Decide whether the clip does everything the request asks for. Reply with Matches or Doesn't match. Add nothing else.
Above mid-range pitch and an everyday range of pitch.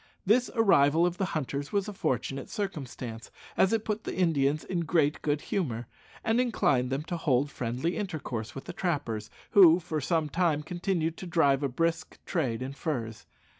Doesn't match